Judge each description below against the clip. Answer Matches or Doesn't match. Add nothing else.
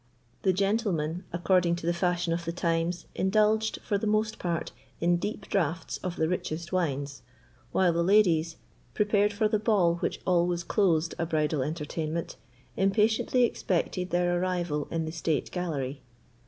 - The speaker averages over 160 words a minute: Doesn't match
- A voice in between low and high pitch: Matches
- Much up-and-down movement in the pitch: Doesn't match